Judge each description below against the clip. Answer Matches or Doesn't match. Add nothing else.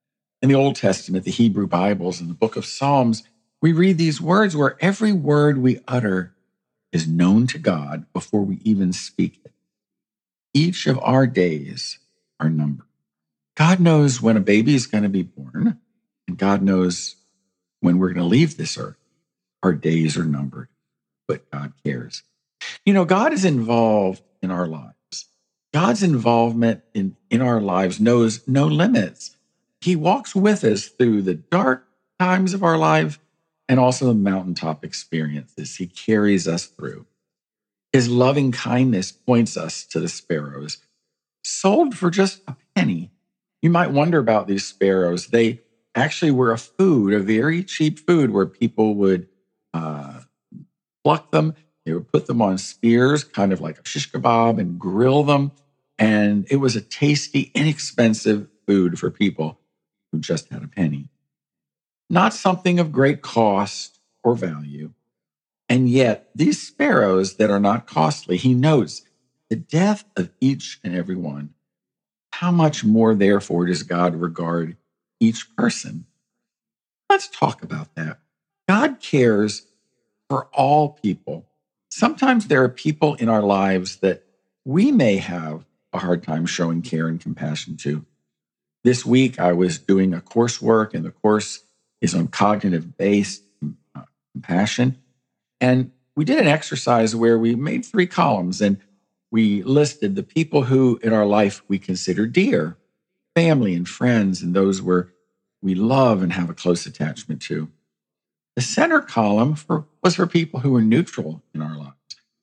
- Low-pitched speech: Matches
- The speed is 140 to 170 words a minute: Matches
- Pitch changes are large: Matches